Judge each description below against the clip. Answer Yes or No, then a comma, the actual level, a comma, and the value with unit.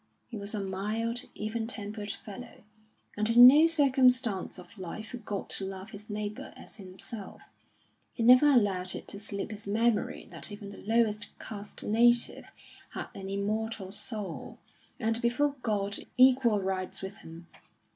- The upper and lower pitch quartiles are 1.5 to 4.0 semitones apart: Yes, average, 2.8 semitones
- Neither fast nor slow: Yes, average, 150 wpm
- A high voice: Yes, high, 215 Hz